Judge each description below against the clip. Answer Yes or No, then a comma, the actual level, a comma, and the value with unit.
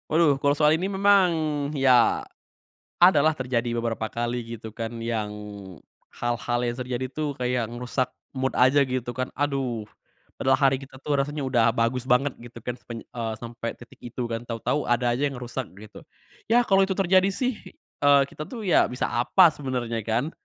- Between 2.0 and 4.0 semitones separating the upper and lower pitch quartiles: Yes, average, 3.7 semitones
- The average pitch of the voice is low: Yes, low, 130 Hz